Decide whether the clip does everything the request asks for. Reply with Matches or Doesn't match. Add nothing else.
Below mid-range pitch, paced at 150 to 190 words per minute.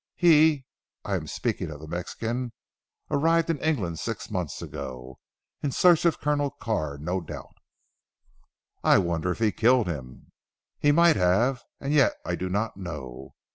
Matches